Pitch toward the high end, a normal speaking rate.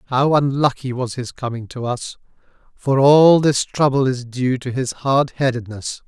No: low, 130 Hz; average, 170 wpm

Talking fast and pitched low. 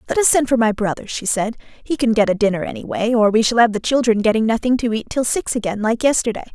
No: fast, 265 wpm; high, 230 Hz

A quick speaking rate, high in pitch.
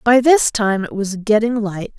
Yes: fast, 210 wpm; high, 220 Hz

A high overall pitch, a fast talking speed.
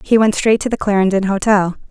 Yes: high, 200 Hz; fast, 220 wpm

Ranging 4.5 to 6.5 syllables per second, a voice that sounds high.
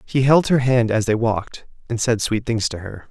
No: 5.0 syllables/s; low, 115 Hz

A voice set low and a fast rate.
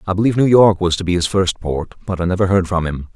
Yes: very low, 90 Hz; fast, 305 wpm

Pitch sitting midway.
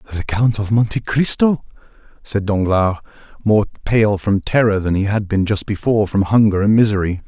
No: low, 105 Hz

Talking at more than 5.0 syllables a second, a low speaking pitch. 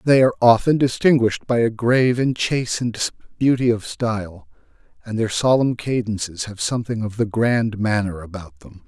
Yes: 5.2 syllables/s; low, 115 Hz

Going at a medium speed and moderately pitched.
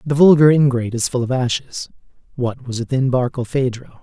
No: average, 165 wpm; low, 130 Hz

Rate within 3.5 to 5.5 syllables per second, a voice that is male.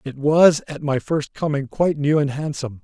Yes: 5.2 syllables/s; male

